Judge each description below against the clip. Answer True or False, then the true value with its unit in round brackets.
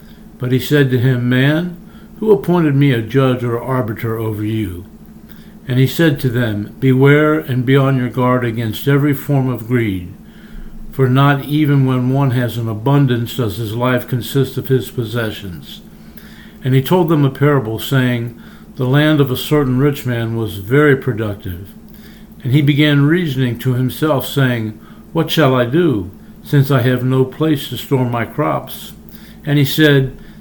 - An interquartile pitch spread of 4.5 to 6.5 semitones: False (3.5 semitones)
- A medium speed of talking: True (170 wpm)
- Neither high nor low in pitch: False (130 Hz)